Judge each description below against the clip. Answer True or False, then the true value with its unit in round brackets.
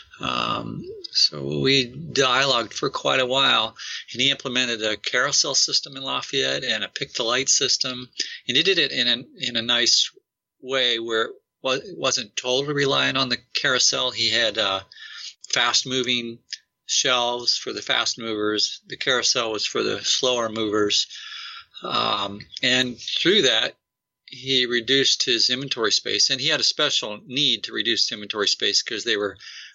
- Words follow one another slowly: False (160 wpm)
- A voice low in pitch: True (125 Hz)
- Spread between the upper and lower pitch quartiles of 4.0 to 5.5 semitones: False (2.8 semitones)